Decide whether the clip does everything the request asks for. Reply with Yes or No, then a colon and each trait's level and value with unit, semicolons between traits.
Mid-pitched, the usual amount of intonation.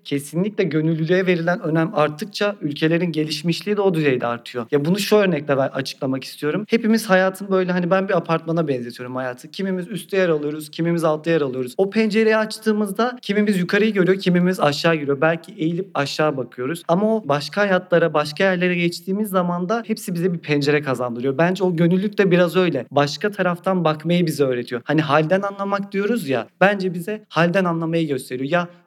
Yes: medium, 175 Hz; average, 4.4 semitones